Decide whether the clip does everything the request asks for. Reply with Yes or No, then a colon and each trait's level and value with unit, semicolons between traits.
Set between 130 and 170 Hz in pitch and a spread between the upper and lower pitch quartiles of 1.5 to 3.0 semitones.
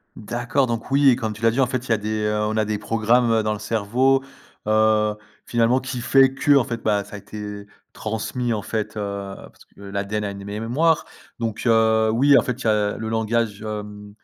No: low, 110 Hz; narrow, 2.4 semitones